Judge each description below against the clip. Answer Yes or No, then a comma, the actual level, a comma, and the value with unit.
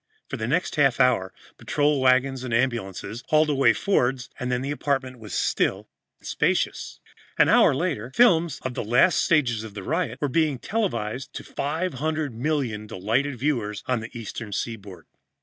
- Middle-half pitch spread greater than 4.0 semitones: Yes, average, 4.5 semitones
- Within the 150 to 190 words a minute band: Yes, average, 165 wpm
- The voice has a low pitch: Yes, low, 130 Hz